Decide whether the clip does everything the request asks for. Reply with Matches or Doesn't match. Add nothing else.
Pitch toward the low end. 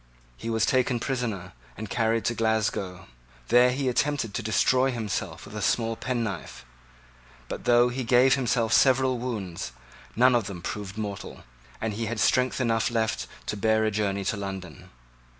Matches